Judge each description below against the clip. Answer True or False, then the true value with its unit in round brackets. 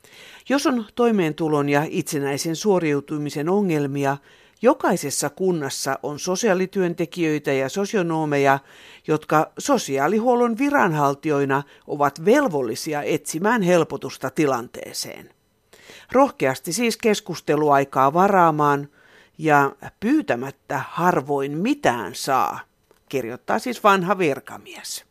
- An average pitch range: False (6.3 semitones)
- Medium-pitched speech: True (160 Hz)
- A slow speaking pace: True (80 wpm)